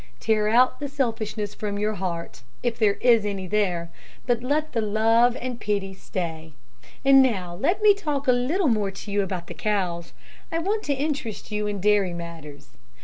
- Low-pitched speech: No, high, 215 Hz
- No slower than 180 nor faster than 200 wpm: Yes, average, 185 wpm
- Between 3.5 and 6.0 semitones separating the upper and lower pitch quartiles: Yes, average, 4.8 semitones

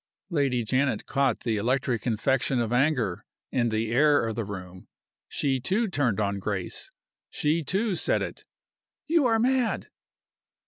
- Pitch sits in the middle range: No, low, 130 Hz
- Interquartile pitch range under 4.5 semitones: No, wide, 5.5 semitones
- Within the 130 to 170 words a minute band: Yes, average, 145 wpm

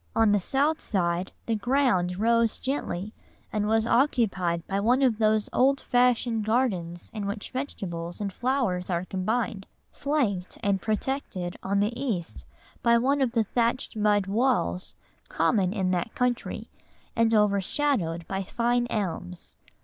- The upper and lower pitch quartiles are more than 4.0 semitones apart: Yes, average, 4.6 semitones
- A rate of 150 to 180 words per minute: No, average, 140 wpm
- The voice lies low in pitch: No, high, 215 Hz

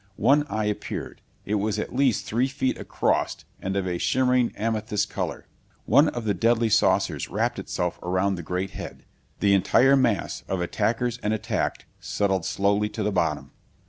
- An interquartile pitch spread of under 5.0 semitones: Yes, average, 3.5 semitones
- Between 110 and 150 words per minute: No, average, 170 wpm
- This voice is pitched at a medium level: No, low, 105 Hz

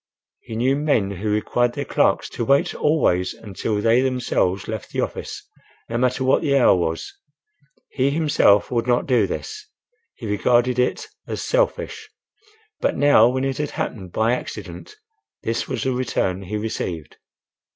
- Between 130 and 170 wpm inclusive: Yes, average, 160 wpm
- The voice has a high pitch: No, low, 120 Hz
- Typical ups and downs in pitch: Yes, average, 4.4 semitones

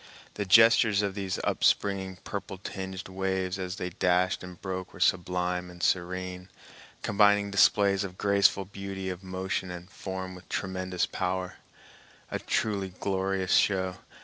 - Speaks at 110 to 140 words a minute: Yes, slow, 135 wpm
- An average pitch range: No, narrow, 1.2 semitones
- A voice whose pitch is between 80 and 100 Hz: Yes, very low, 95 Hz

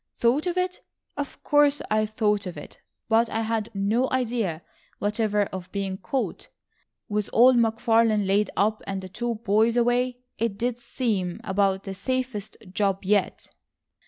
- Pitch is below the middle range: No, high, 220 Hz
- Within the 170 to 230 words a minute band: No, average, 155 wpm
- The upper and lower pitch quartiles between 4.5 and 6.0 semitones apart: No, average, 3.4 semitones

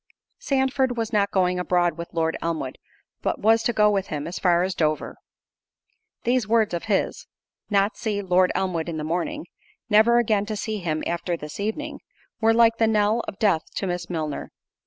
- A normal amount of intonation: Yes, average, 4.4 semitones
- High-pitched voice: Yes, high, 200 Hz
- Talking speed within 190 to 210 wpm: No, average, 180 wpm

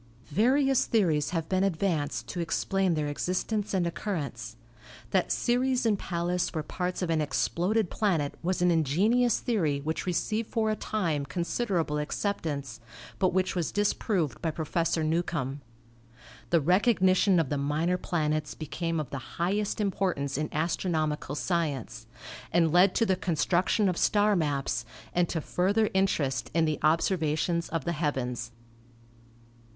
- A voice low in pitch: No, medium, 170 Hz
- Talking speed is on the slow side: No, average, 145 wpm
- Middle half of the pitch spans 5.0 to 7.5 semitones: No, average, 4.3 semitones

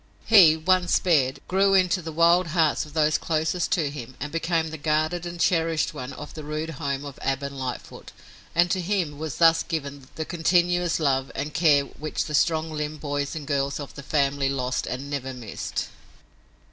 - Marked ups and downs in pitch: No, average, 3.0 semitones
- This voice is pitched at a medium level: Yes, medium, 155 Hz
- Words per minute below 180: No, average, 190 wpm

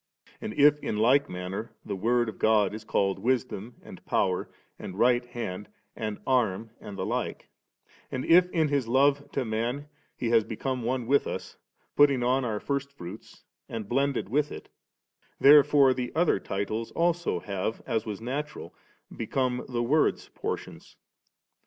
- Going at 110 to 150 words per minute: No, average, 160 wpm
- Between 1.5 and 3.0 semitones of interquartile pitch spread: No, average, 4.4 semitones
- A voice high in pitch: No, low, 120 Hz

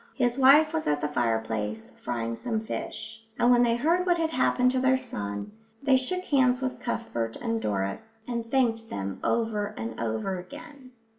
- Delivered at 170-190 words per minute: Yes, average, 175 wpm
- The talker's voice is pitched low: No, high, 230 Hz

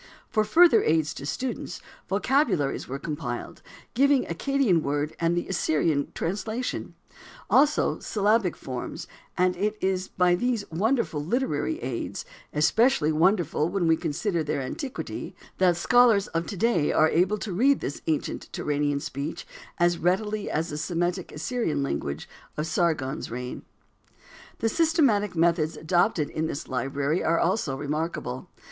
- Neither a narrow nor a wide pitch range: No, wide, 6.0 semitones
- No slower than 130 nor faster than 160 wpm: Yes, average, 140 wpm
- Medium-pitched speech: Yes, medium, 175 Hz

